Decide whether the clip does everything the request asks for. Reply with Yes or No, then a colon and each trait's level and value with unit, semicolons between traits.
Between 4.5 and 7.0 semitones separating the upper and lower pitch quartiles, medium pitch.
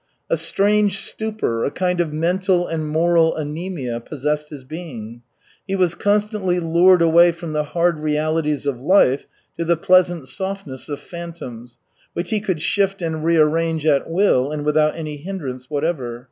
No: average, 3.2 semitones; medium, 165 Hz